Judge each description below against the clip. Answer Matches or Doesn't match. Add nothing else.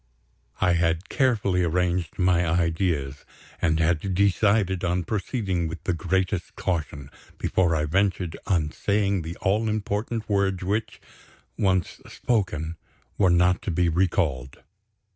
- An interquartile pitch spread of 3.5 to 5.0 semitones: Doesn't match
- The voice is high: Doesn't match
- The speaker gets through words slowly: Matches